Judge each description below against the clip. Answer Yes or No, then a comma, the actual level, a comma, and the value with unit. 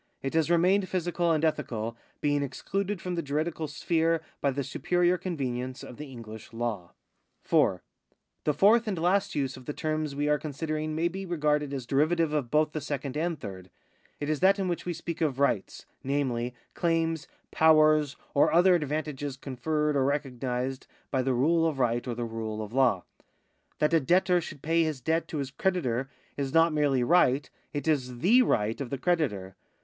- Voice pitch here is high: No, medium, 150 Hz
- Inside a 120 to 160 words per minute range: No, average, 185 wpm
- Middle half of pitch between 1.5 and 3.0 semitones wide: No, average, 4.1 semitones